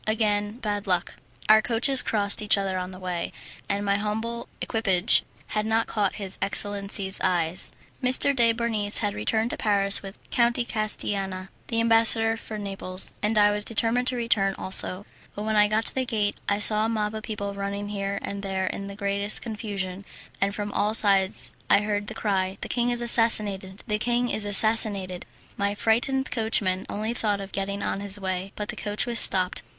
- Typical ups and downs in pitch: No, narrow, 2.1 semitones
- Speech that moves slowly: No, average, 190 wpm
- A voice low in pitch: No, high, 205 Hz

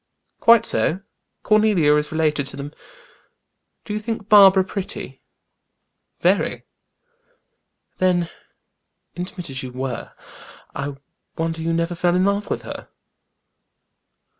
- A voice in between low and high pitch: Yes, medium, 175 Hz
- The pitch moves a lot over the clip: No, average, 5.0 semitones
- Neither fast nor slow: No, slow, 115 wpm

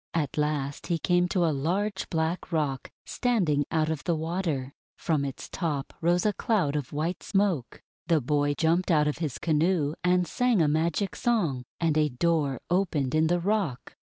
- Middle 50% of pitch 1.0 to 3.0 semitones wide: No, average, 3.4 semitones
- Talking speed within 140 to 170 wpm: No, average, 180 wpm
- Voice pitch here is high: No, medium, 160 Hz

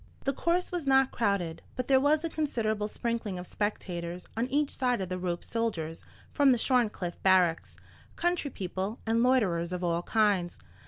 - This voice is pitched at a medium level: No, high, 220 Hz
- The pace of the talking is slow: No, average, 165 wpm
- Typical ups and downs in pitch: No, wide, 6.5 semitones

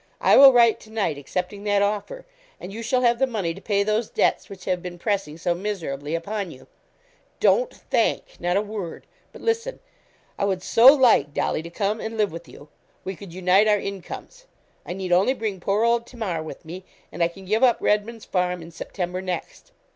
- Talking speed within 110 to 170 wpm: No, fast, 205 wpm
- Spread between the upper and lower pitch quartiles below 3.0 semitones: No, average, 4.0 semitones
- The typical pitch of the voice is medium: No, high, 200 Hz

